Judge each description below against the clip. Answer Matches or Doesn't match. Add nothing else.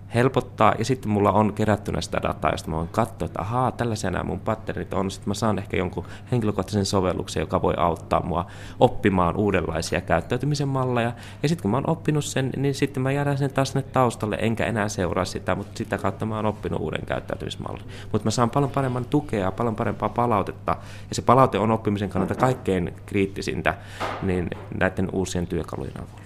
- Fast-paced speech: Matches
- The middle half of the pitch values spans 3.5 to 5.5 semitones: Matches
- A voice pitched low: Matches